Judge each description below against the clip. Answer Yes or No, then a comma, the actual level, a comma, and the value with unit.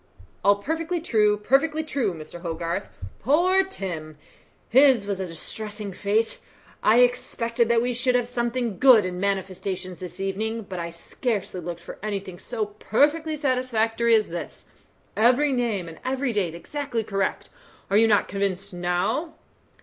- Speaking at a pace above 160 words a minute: No, average, 150 wpm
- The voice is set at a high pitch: Yes, high, 215 Hz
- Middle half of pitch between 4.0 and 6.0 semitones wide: Yes, average, 4.9 semitones